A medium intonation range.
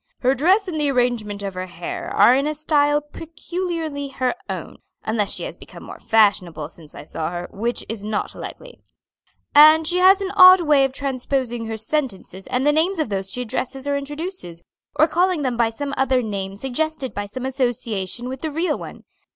No: wide, 6.0 semitones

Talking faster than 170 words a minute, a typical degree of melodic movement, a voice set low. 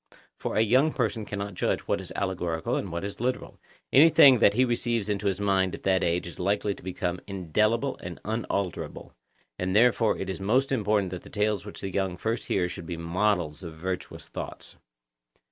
Yes: average, 195 wpm; average, 3.2 semitones; low, 100 Hz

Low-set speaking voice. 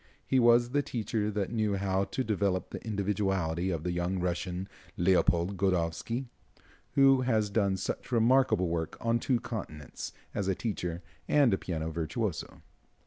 Yes: low, 100 Hz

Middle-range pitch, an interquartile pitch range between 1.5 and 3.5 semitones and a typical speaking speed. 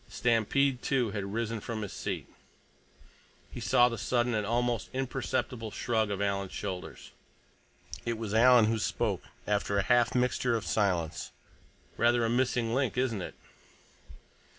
No: low, 115 Hz; average, 2.8 semitones; average, 145 wpm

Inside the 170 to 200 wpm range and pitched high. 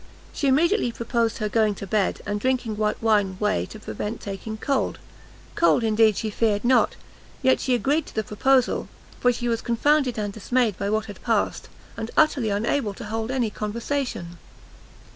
Yes: average, 175 wpm; high, 225 Hz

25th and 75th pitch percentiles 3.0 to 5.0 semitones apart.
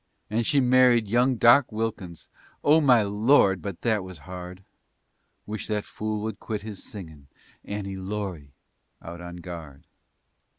Yes: average, 4.0 semitones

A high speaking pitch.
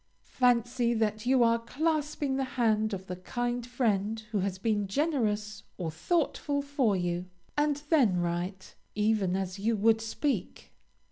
Yes: high, 225 Hz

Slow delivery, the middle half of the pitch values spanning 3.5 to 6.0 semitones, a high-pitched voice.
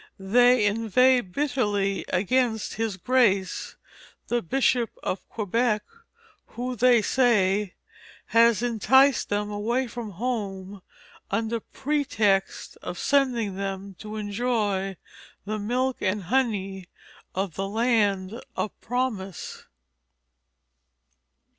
Yes: slow, 95 wpm; average, 3.8 semitones; high, 215 Hz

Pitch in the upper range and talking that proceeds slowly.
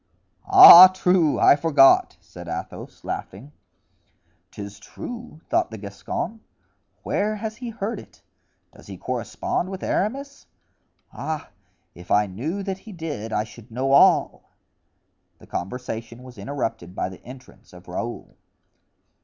No: medium, 140 Hz; slow, 130 wpm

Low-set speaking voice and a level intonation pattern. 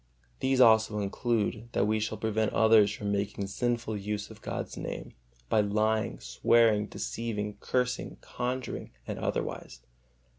Yes: low, 110 Hz; narrow, 2.2 semitones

